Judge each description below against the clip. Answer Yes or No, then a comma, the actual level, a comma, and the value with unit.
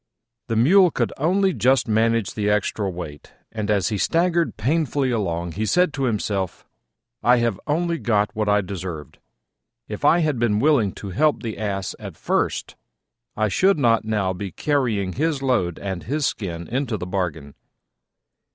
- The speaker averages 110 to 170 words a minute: Yes, average, 165 wpm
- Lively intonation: Yes, wide, 6.4 semitones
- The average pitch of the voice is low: Yes, low, 110 Hz